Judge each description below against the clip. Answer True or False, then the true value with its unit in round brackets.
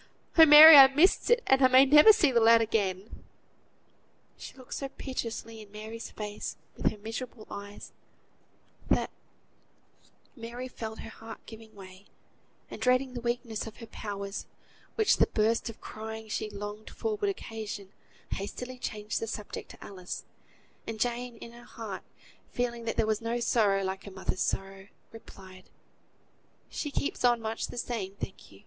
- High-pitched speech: True (225 Hz)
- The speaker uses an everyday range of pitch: True (3.2 semitones)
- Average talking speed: True (165 wpm)